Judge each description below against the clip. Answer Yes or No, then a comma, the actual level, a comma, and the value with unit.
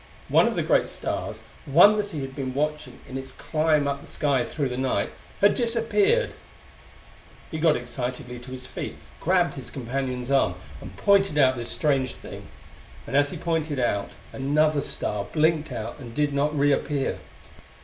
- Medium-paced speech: Yes, average, 170 wpm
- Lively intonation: No, average, 3.2 semitones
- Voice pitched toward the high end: No, medium, 145 Hz